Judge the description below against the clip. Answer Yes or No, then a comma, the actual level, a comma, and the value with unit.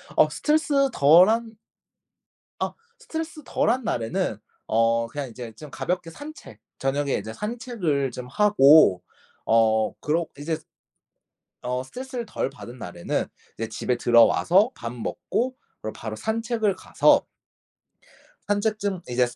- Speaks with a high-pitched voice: No, medium, 155 Hz